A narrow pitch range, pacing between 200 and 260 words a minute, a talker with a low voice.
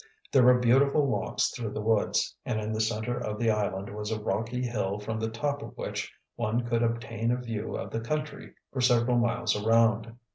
Yes: narrow, 2.2 semitones; fast, 205 wpm; low, 115 Hz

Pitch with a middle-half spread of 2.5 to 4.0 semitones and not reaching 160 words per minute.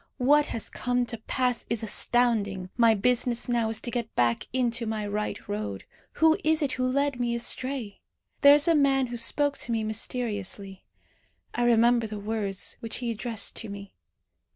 No: average, 2.9 semitones; average, 175 wpm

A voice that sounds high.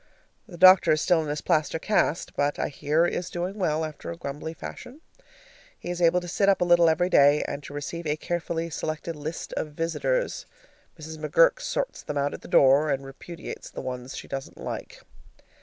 No: medium, 160 Hz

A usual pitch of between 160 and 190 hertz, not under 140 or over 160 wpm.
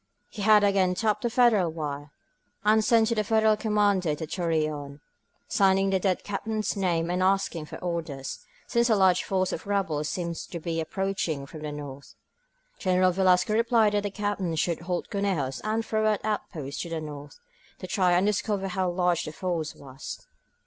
No: medium, 185 Hz; average, 180 wpm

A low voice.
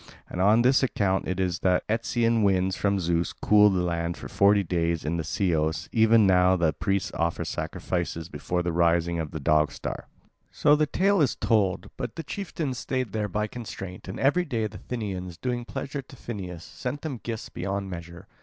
Yes: very low, 95 Hz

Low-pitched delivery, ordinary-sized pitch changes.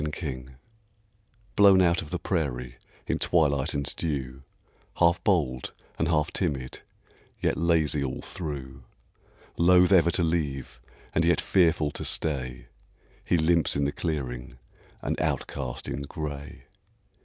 Yes: very low, 75 Hz; average, 4.0 semitones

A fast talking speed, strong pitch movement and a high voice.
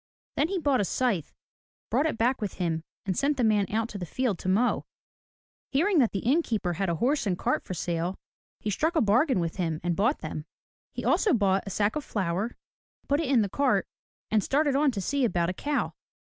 Yes: fast, 225 wpm; wide, 7.0 semitones; high, 215 Hz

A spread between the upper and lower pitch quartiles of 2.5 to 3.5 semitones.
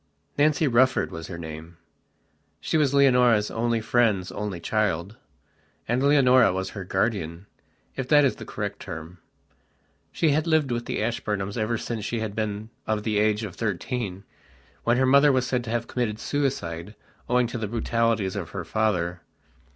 No: average, 4.3 semitones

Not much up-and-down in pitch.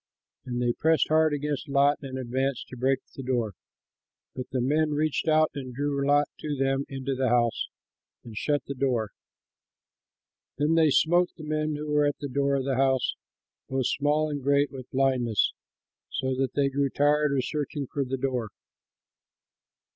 Yes: narrow, 2.2 semitones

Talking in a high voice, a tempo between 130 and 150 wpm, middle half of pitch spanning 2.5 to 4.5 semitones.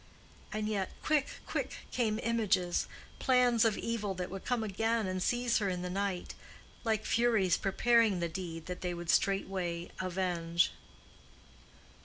Yes: high, 195 Hz; average, 145 wpm; average, 4.1 semitones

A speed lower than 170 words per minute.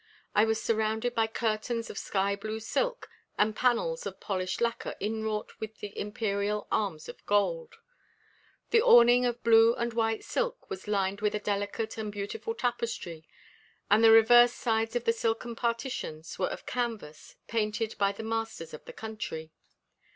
Yes: average, 160 wpm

